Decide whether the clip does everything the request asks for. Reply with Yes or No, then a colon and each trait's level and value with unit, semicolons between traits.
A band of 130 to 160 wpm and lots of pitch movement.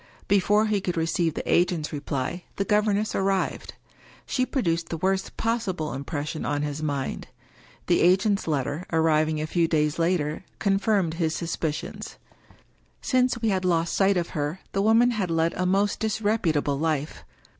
No: average, 155 wpm; average, 4.4 semitones